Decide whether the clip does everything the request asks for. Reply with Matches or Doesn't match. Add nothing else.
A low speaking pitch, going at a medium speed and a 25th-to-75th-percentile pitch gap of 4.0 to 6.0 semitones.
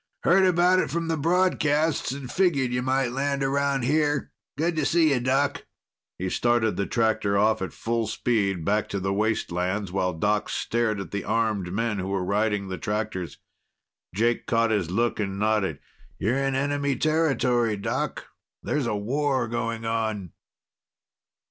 Matches